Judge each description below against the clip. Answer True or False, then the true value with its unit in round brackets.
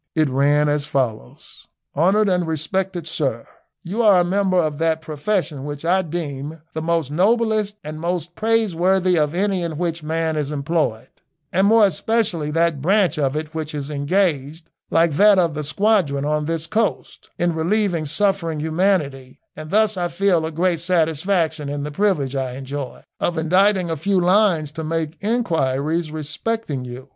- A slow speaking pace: False (165 wpm)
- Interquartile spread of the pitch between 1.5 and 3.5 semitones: False (4.0 semitones)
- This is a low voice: False (165 Hz)